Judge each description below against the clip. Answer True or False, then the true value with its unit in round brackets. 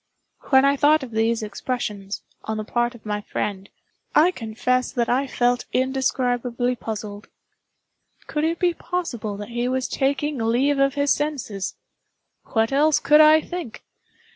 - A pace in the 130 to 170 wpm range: True (150 wpm)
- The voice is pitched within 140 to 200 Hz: False (250 Hz)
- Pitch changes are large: False (4.3 semitones)